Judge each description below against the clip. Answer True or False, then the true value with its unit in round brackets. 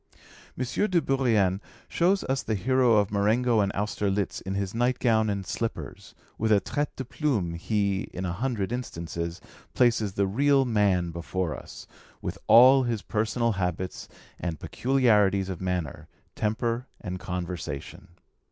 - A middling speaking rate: True (145 wpm)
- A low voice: True (105 Hz)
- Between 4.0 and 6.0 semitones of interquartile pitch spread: True (4.7 semitones)